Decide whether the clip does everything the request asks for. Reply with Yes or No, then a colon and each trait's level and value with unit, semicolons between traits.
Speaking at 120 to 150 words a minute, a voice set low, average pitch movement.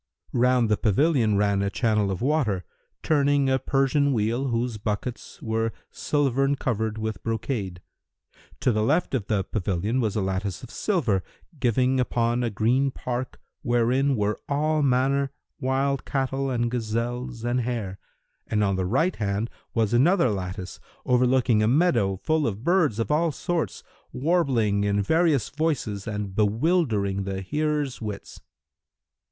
Yes: average, 145 wpm; low, 120 Hz; average, 4.6 semitones